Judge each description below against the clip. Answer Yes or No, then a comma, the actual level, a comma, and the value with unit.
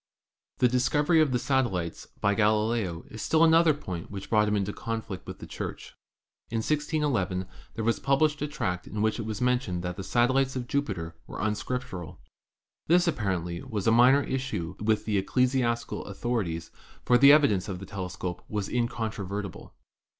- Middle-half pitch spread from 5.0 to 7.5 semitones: Yes, average, 5.3 semitones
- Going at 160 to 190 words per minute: Yes, average, 180 wpm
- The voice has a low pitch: Yes, low, 110 Hz